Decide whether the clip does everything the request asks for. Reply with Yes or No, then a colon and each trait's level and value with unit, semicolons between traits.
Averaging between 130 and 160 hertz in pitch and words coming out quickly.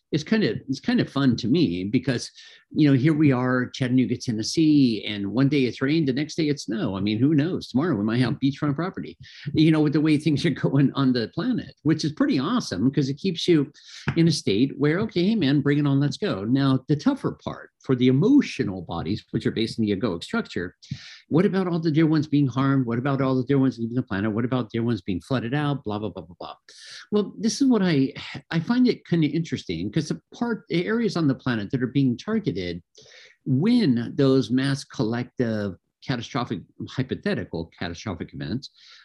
Yes: low, 135 Hz; fast, 220 wpm